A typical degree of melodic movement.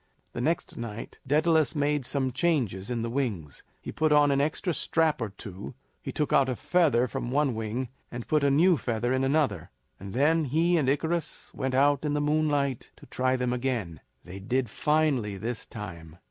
Yes: average, 4.4 semitones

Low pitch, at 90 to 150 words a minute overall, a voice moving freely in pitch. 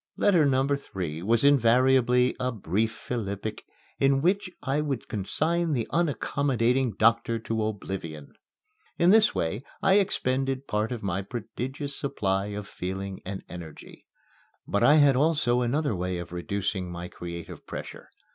Yes: low, 115 Hz; average, 140 wpm; wide, 5.9 semitones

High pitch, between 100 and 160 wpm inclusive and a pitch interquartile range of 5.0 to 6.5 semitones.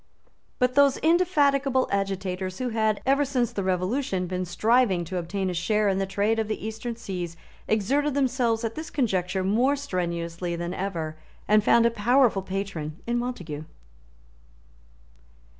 Yes: high, 210 Hz; average, 150 wpm; wide, 5.5 semitones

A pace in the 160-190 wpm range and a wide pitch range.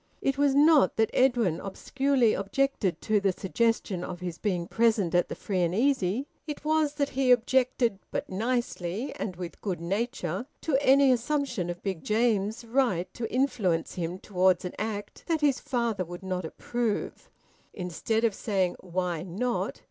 Yes: average, 165 wpm; wide, 5.9 semitones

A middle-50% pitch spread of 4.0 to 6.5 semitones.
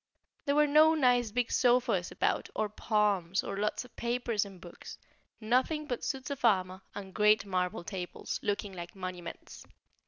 Yes: average, 4.8 semitones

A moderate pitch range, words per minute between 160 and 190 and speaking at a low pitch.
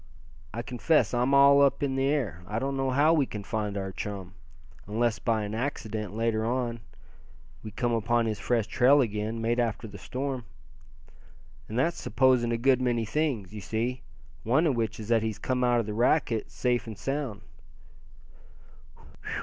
Yes: average, 3.1 semitones; average, 175 wpm; low, 120 Hz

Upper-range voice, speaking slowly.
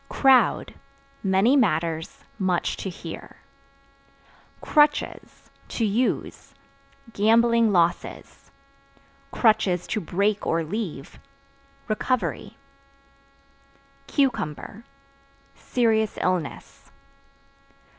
Yes: high, 210 Hz; slow, 65 wpm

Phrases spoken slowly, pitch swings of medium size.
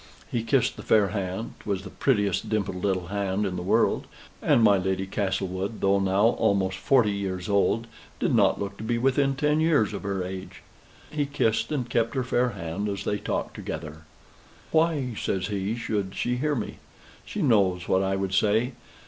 No: average, 185 wpm; average, 3.8 semitones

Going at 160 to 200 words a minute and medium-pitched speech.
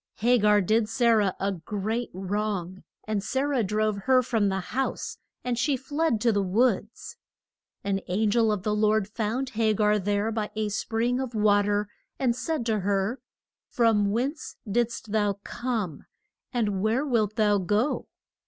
No: average, 170 wpm; high, 215 Hz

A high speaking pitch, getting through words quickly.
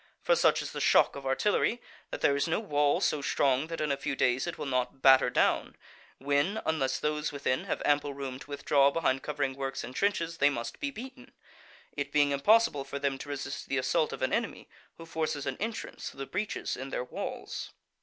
No: medium, 140 Hz; fast, 215 wpm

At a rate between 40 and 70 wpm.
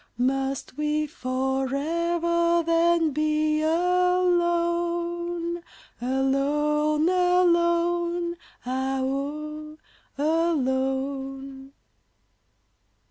Yes: slow, 50 wpm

